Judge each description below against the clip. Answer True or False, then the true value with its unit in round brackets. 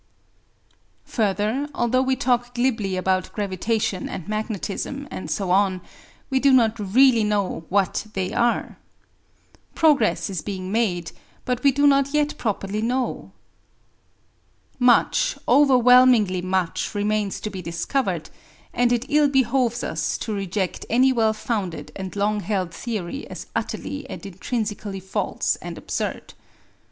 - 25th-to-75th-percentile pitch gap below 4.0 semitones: False (4.8 semitones)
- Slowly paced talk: True (130 wpm)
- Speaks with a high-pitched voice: True (215 Hz)